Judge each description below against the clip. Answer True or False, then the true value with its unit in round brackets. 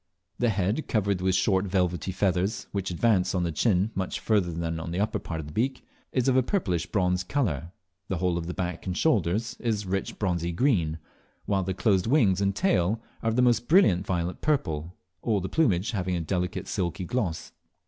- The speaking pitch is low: True (95 Hz)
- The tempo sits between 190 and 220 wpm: True (200 wpm)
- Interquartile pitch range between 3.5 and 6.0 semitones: True (3.9 semitones)